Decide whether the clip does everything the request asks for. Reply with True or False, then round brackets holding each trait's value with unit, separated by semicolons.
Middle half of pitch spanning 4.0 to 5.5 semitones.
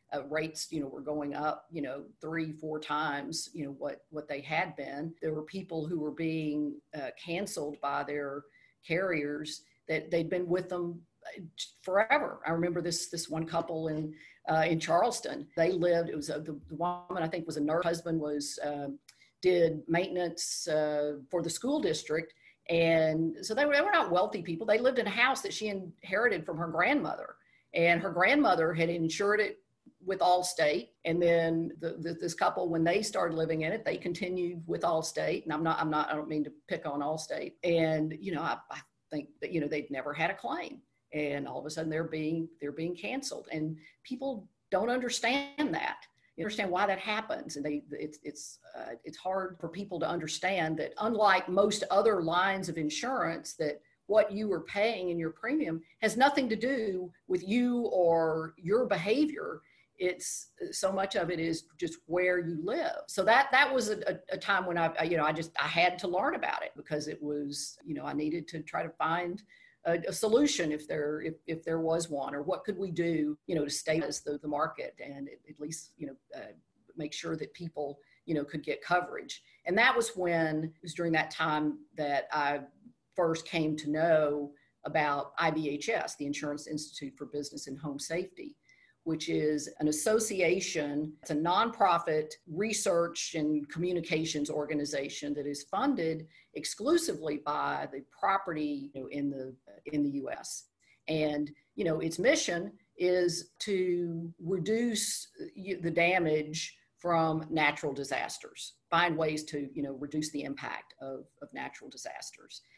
False (3.1 semitones)